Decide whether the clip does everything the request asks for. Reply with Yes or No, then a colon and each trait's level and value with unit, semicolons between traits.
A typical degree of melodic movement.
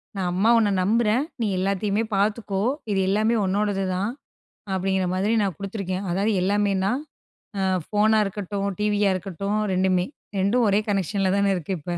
No: narrow, 1.7 semitones